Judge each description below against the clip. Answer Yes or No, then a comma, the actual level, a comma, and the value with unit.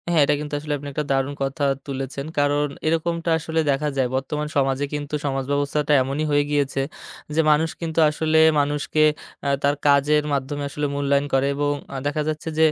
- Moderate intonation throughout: No, narrow, 1.5 semitones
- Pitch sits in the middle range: Yes, medium, 145 Hz